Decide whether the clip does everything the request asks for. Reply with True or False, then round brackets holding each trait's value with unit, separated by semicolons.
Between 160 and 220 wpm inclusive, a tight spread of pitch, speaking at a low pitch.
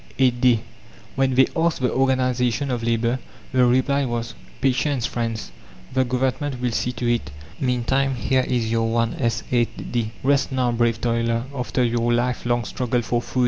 True (165 wpm; 1.8 semitones; 125 Hz)